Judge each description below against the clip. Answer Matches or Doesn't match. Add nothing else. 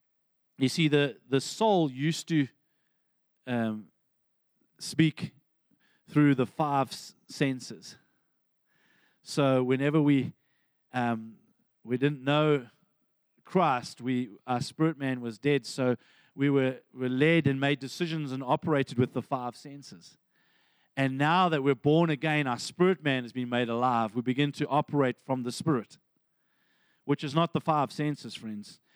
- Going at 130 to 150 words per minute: Matches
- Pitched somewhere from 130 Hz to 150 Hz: Matches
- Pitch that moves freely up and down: Doesn't match